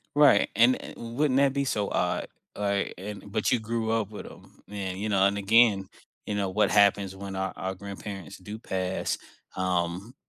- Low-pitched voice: Yes, low, 100 Hz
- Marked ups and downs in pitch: No, average, 2.8 semitones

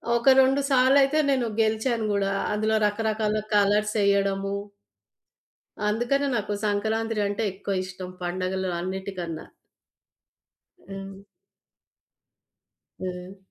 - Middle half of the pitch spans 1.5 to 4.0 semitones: Yes, narrow, 2.5 semitones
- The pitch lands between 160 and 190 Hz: No, high, 205 Hz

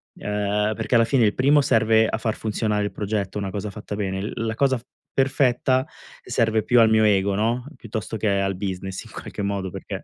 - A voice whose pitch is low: Yes, low, 110 Hz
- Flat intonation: Yes, narrow, 2.3 semitones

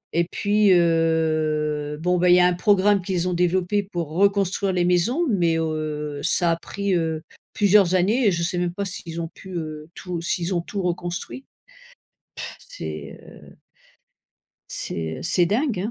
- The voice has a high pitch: No, medium, 175 Hz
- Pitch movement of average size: Yes, average, 3.1 semitones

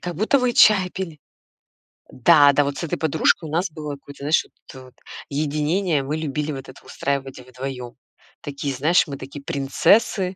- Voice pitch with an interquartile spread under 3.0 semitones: No, average, 3.5 semitones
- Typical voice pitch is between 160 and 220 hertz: No, medium, 145 Hz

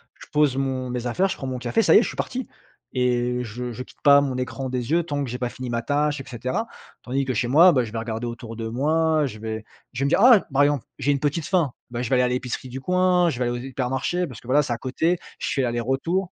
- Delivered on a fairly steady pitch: No, average, 3.3 semitones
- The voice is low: Yes, low, 130 Hz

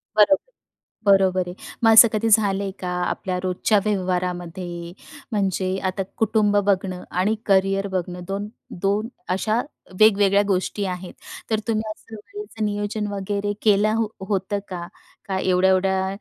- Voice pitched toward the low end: No, high, 195 Hz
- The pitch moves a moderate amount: No, narrow, 2.1 semitones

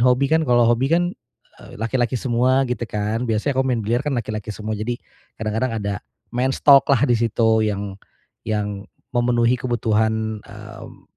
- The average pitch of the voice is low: Yes, low, 120 Hz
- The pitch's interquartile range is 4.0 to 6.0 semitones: No, average, 2.8 semitones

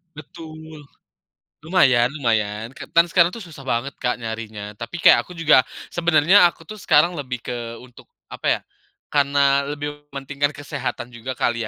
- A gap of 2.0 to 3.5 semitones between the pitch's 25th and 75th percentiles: No, average, 4.7 semitones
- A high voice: No, medium, 140 Hz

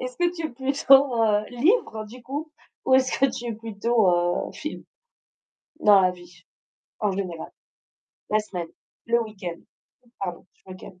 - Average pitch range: No, wide, 5.8 semitones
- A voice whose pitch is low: No, high, 220 Hz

